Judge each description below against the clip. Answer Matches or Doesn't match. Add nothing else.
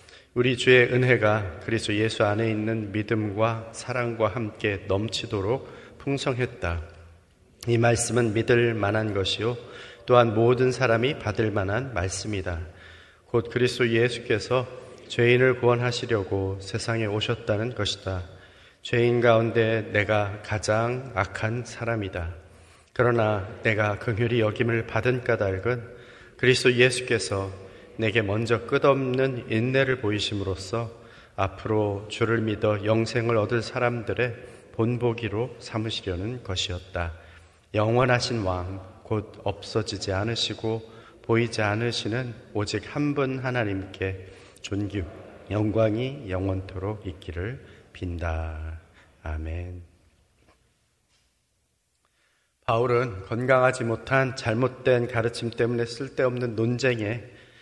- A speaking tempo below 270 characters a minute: Matches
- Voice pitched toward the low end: Matches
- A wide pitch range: Doesn't match